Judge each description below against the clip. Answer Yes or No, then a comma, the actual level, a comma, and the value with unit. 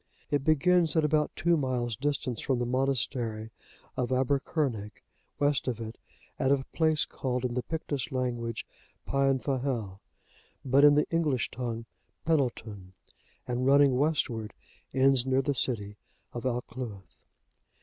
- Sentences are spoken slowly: Yes, slow, 130 wpm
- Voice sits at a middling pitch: No, low, 130 Hz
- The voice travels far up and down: No, average, 3.1 semitones